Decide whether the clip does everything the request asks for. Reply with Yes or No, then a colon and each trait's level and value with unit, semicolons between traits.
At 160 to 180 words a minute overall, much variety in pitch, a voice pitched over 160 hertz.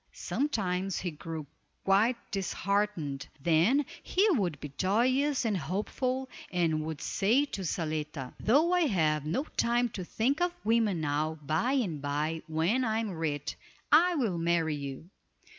No: average, 145 wpm; wide, 7.5 semitones; medium, 185 Hz